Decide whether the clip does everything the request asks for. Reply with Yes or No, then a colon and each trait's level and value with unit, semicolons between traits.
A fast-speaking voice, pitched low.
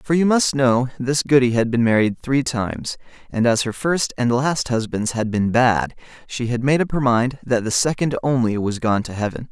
Yes: fast, 220 wpm; low, 125 Hz